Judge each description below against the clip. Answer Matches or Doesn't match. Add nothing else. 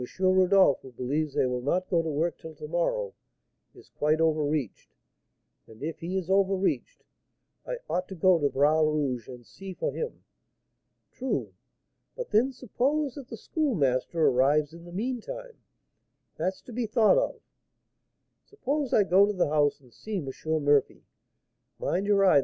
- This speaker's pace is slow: Doesn't match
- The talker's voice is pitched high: Doesn't match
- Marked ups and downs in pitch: Matches